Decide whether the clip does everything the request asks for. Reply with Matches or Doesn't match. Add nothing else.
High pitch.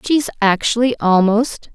Matches